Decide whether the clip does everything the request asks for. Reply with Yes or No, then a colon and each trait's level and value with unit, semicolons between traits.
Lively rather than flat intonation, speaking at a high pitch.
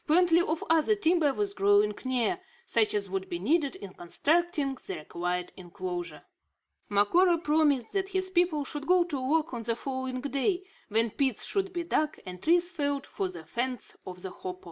Yes: wide, 8.8 semitones; very high, 270 Hz